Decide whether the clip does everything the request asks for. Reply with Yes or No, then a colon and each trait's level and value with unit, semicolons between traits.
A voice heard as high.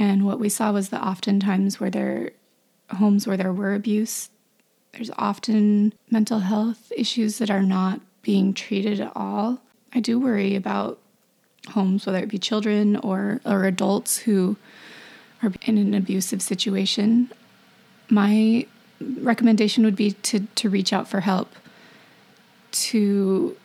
Yes: high, 210 Hz